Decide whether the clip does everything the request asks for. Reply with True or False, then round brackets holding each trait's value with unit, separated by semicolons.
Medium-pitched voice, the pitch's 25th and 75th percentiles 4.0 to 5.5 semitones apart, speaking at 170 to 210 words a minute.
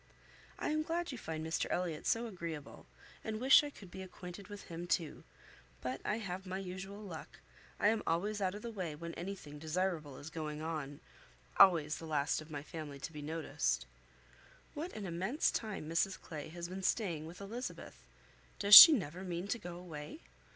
True (180 Hz; 4.3 semitones; 190 wpm)